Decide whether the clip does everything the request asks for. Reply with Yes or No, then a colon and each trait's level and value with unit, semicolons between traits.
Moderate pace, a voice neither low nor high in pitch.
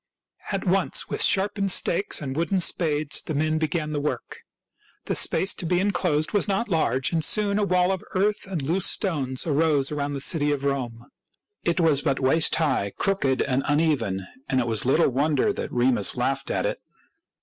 Yes: average, 190 wpm; medium, 155 Hz